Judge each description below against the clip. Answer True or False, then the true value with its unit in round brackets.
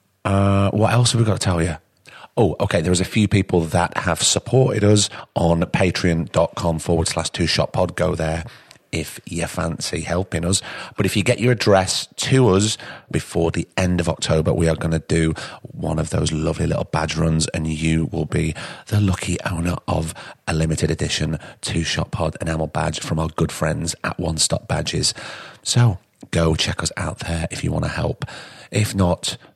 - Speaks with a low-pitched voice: True (90 Hz)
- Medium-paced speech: True (195 wpm)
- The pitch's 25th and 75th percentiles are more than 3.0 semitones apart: True (4.0 semitones)